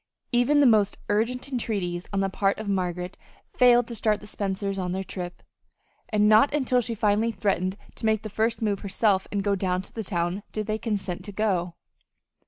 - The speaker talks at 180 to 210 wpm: Yes, average, 195 wpm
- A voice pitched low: No, high, 205 Hz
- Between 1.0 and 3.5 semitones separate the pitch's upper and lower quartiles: Yes, average, 2.7 semitones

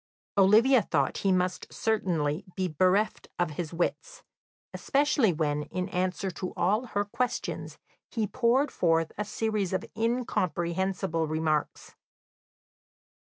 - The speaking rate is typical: No, slow, 115 wpm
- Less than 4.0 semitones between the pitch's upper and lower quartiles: No, average, 4.6 semitones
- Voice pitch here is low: No, medium, 185 Hz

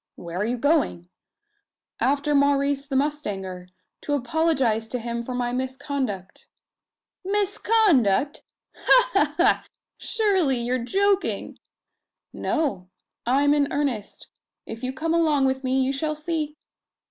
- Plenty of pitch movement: No, average, 4.1 semitones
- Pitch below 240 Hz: No, very high, 280 Hz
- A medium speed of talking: No, slow, 125 wpm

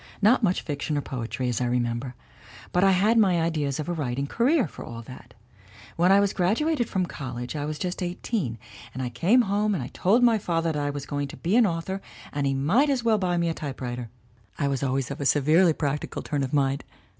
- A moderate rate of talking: No, fast, 225 wpm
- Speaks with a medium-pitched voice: Yes, medium, 155 Hz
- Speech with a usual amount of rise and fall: No, wide, 6.2 semitones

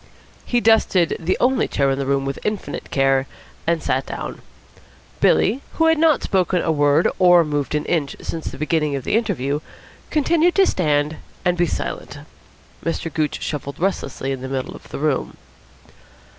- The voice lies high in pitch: No, medium, 160 Hz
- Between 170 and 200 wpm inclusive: Yes, average, 175 wpm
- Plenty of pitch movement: Yes, wide, 5.7 semitones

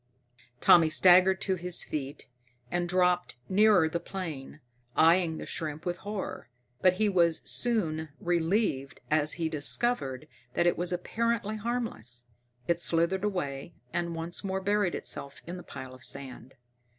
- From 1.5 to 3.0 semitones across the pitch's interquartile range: No, average, 3.4 semitones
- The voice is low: No, medium, 175 Hz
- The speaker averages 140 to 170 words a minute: Yes, average, 145 wpm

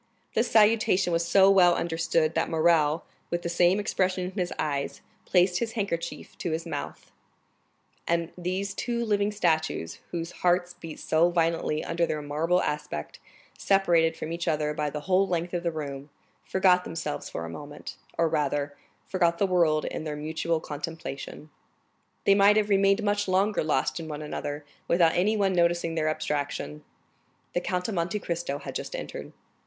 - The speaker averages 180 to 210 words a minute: No, average, 170 wpm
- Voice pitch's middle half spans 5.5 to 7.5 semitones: No, average, 3.2 semitones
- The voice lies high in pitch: No, medium, 170 Hz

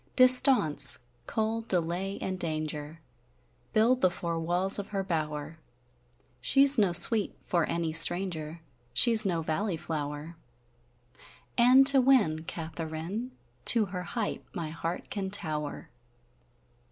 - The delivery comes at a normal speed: No, slow, 125 wpm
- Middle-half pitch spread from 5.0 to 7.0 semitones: Yes, average, 5.3 semitones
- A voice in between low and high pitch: Yes, medium, 175 Hz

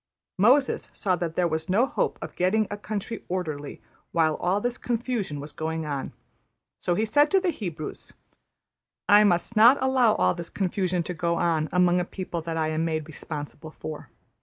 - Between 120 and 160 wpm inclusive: No, average, 185 wpm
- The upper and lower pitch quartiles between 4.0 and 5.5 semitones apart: Yes, average, 5.1 semitones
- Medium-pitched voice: Yes, medium, 180 Hz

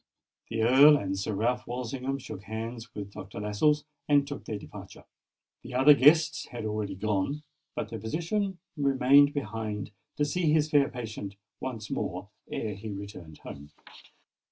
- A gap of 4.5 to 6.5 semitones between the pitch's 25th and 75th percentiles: Yes, average, 5.3 semitones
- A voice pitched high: No, low, 120 Hz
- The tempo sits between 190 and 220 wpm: No, average, 155 wpm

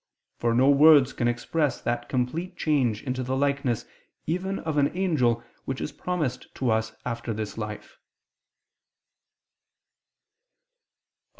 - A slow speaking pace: Yes, slow, 120 wpm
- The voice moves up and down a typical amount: Yes, average, 4.4 semitones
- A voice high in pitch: No, low, 130 Hz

